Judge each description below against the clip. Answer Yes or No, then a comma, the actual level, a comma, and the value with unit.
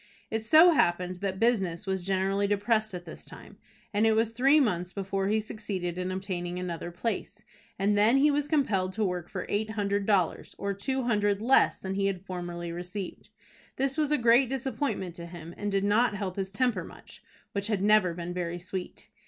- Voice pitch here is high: Yes, high, 200 Hz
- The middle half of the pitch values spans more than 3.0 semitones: Yes, average, 3.5 semitones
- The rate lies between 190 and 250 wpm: Yes, average, 195 wpm